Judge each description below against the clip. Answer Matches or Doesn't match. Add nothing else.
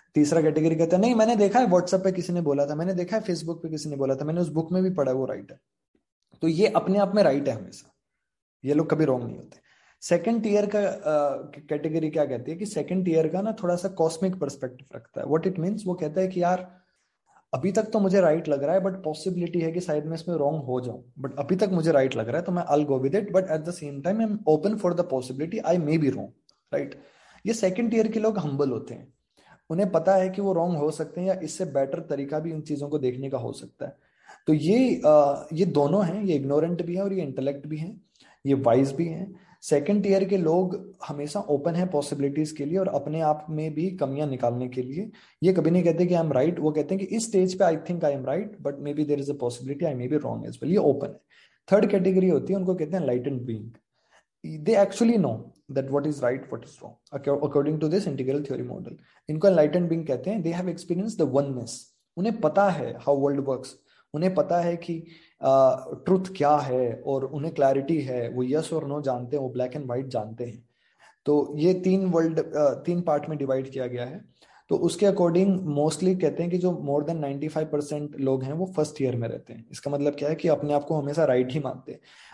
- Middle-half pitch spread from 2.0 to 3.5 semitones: Doesn't match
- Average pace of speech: Doesn't match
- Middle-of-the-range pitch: Matches